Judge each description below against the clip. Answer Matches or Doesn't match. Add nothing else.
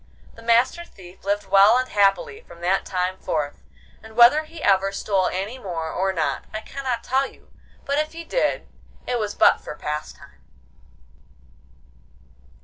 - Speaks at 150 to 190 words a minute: Matches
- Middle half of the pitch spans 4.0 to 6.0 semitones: Matches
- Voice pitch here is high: Matches